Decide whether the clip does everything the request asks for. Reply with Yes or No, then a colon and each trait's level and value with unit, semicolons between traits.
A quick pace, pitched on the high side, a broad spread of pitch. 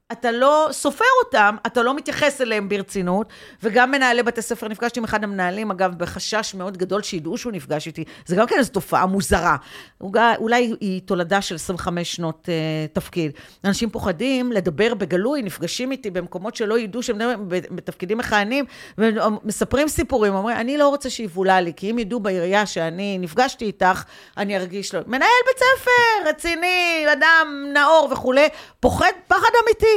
Yes: fast, 160 wpm; high, 220 Hz; wide, 5.9 semitones